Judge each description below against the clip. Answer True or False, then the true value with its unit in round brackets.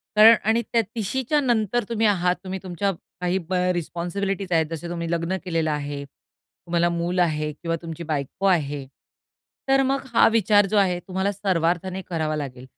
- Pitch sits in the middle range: True (180 Hz)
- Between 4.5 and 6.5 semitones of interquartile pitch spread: False (3.3 semitones)